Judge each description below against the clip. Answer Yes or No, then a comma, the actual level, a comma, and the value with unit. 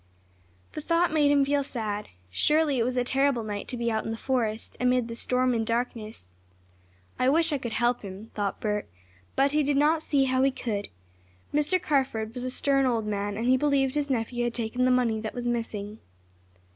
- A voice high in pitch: Yes, very high, 250 Hz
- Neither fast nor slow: No, fast, 210 wpm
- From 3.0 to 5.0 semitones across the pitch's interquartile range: Yes, average, 3.7 semitones